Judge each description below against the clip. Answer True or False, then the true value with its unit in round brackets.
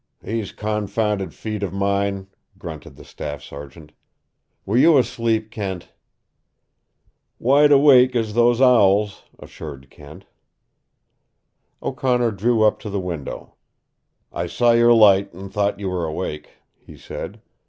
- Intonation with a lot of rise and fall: False (3.7 semitones)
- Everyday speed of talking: False (125 wpm)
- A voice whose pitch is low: True (105 Hz)